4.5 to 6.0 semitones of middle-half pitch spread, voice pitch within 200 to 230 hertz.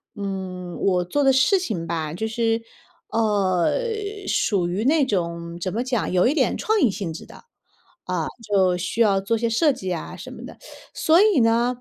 Yes: average, 5.0 semitones; high, 205 Hz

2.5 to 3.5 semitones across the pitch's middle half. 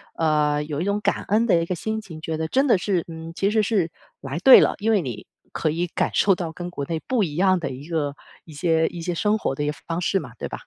No: average, 4.1 semitones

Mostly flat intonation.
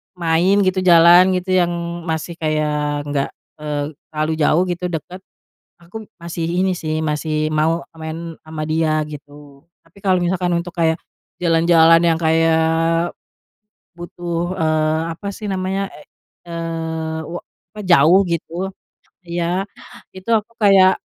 Yes: narrow, 2.0 semitones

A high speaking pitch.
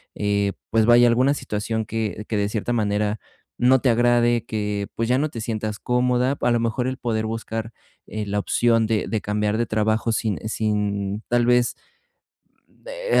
No: low, 115 Hz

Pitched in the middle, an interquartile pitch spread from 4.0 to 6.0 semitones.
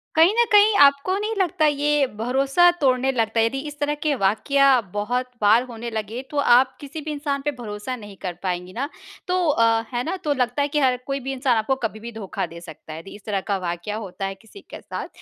No: very high, 255 Hz; average, 5.3 semitones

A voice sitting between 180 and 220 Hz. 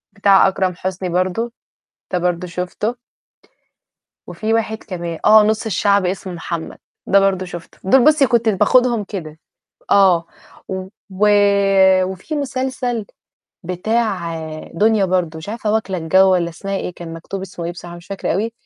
Yes: high, 190 Hz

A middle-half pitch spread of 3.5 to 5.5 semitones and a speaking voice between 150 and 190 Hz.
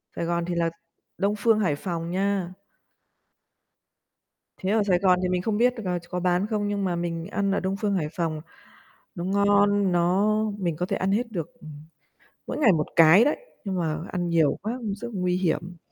No: average, 2.9 semitones; medium, 185 Hz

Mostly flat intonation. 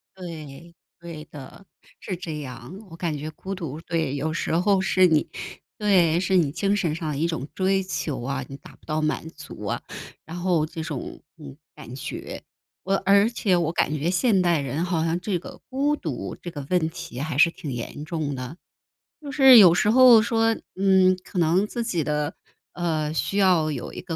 No: average, 3.8 semitones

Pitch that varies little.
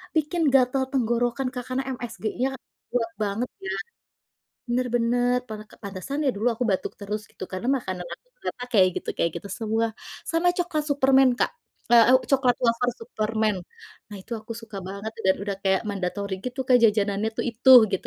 No: average, 3.7 semitones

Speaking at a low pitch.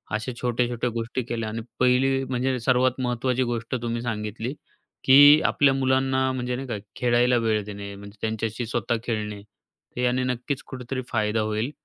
Yes: low, 120 Hz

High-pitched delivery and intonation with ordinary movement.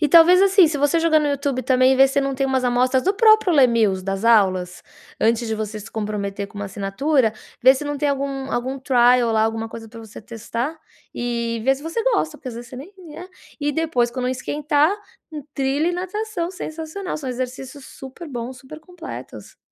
Yes: very high, 265 Hz; average, 4.9 semitones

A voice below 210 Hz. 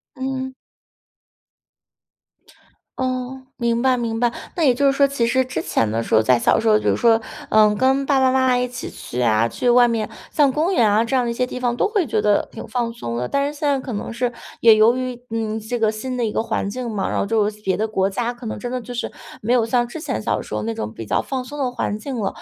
No: high, 240 Hz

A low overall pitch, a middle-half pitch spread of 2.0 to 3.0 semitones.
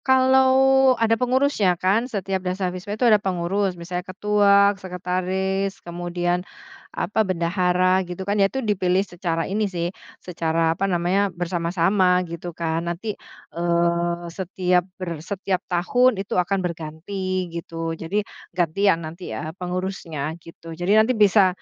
No: medium, 185 Hz; average, 2.7 semitones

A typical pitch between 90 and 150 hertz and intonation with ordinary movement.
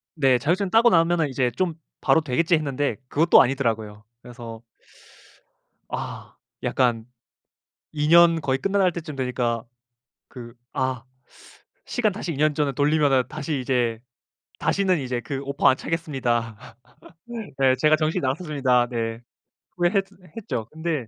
Yes: medium, 140 Hz; average, 4.9 semitones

